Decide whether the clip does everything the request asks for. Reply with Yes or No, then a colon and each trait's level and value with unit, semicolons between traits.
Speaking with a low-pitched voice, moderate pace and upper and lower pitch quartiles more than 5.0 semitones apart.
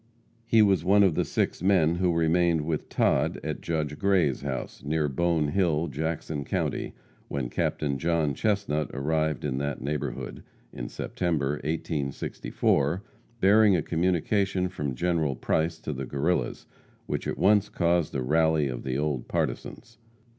No: very low, 80 Hz; average, 145 wpm; average, 3.7 semitones